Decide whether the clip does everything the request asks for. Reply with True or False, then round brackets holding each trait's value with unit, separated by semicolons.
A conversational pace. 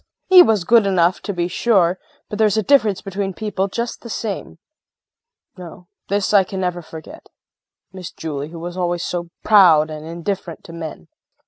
True (175 wpm)